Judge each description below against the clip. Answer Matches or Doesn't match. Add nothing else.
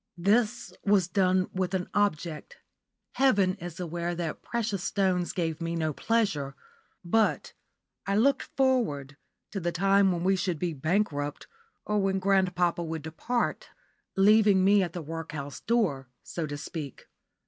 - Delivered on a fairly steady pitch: Doesn't match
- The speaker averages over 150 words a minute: Doesn't match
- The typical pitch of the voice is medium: Matches